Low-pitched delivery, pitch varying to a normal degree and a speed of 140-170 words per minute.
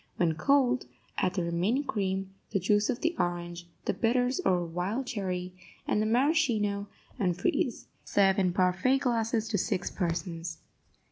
No: high, 195 Hz; average, 4.9 semitones; average, 150 wpm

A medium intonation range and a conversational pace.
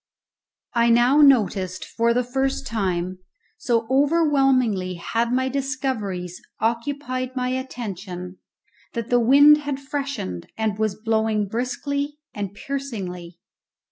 No: average, 4.9 semitones; slow, 110 wpm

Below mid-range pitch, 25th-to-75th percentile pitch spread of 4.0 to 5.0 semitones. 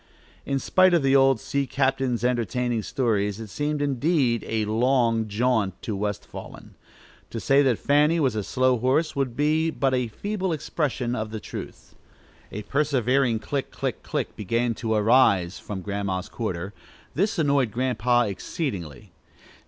Yes: low, 125 Hz; average, 4.4 semitones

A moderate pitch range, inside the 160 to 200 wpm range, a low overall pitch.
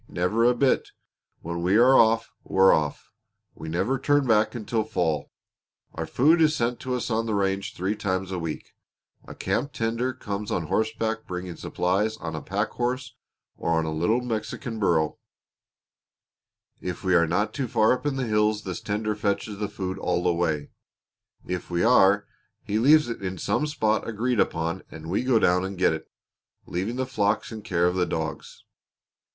Yes: average, 4.4 semitones; average, 180 wpm; low, 105 Hz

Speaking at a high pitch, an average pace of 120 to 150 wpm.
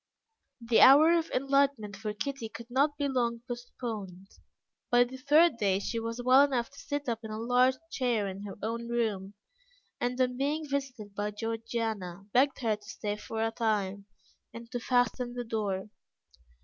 No: high, 235 Hz; average, 175 wpm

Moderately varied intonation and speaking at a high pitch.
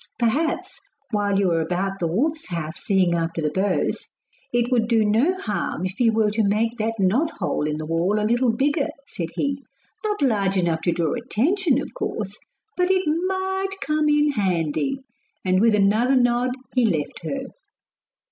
No: wide, 7.1 semitones; high, 225 Hz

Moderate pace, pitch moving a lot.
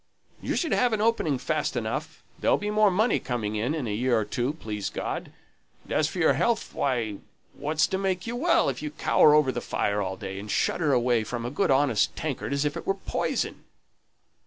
No: fast, 215 wpm; wide, 7.6 semitones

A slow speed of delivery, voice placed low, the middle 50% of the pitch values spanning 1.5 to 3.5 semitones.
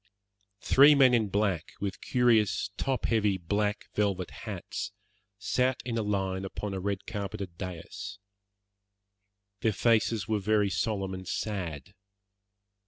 Yes: slow, 125 wpm; low, 105 Hz; narrow, 2.6 semitones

